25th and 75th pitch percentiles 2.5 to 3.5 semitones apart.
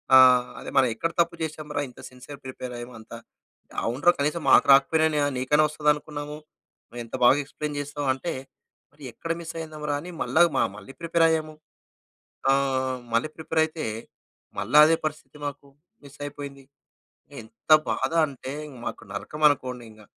Yes: average, 3.0 semitones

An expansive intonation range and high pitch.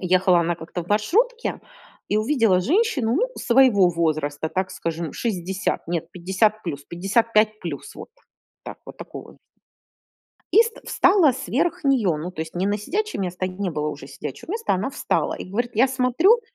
Yes: wide, 6.9 semitones; high, 200 Hz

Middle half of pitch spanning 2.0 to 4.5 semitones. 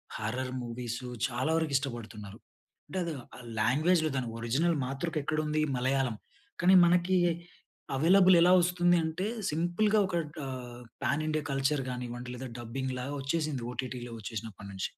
No: average, 5.1 semitones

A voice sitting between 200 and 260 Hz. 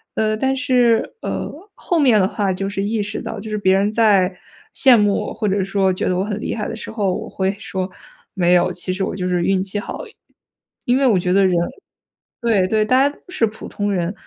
Yes: high, 205 Hz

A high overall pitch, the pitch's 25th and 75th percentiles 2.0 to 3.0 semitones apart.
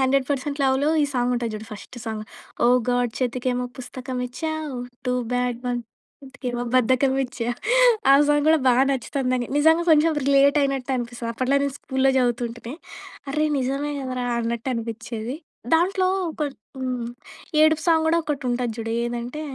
Yes: very high, 255 Hz; narrow, 2.6 semitones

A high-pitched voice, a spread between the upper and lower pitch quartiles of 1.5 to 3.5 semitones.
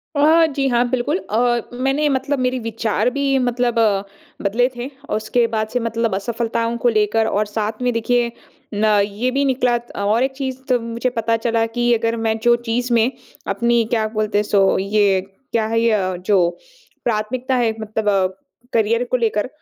Yes: high, 230 Hz; narrow, 2.4 semitones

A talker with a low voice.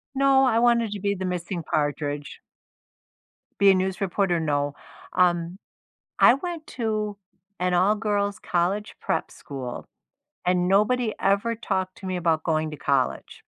No: high, 190 Hz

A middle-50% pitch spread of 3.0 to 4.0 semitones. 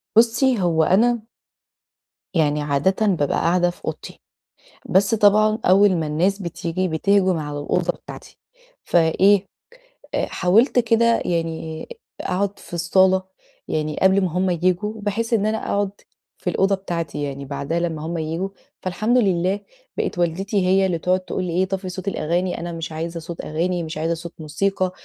Yes: average, 3.3 semitones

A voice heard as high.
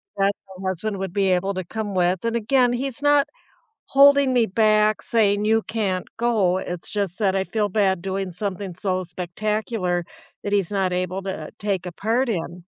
Yes: high, 200 Hz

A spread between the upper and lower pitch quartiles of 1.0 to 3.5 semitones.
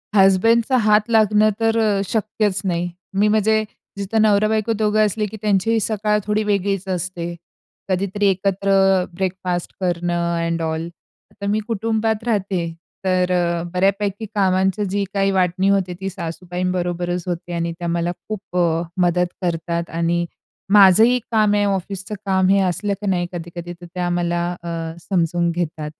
Yes: average, 3.1 semitones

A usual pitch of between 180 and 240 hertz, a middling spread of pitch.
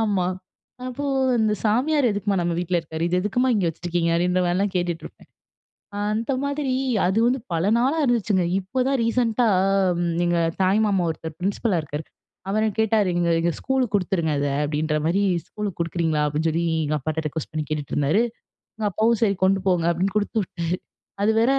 Yes: high, 190 Hz; average, 4.7 semitones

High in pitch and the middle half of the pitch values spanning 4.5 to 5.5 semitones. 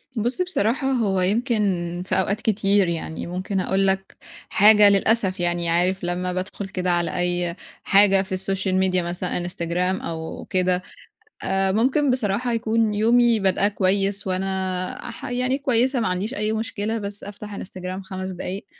No: high, 195 Hz; average, 2.9 semitones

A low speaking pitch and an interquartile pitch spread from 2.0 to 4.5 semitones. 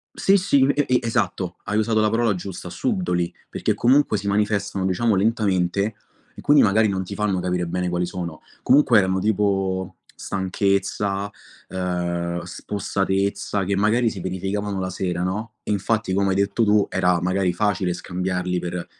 Yes: low, 100 Hz; narrow, 2.6 semitones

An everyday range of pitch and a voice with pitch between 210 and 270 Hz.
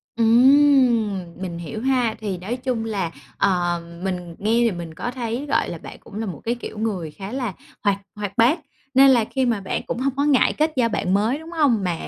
Yes: average, 5.0 semitones; high, 225 Hz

